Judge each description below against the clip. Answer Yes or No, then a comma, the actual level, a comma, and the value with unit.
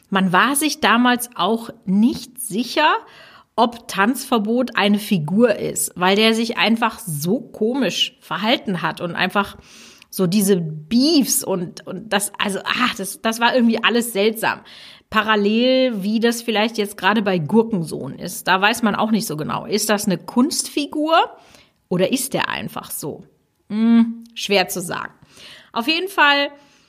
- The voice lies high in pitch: Yes, high, 225 Hz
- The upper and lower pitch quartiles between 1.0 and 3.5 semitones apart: No, average, 3.9 semitones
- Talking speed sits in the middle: Yes, average, 150 wpm